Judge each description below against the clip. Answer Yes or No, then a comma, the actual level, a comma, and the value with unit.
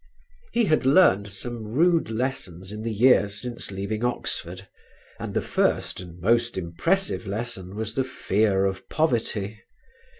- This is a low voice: Yes, low, 110 Hz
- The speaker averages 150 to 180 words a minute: No, average, 140 wpm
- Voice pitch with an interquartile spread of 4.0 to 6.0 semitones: Yes, average, 4.3 semitones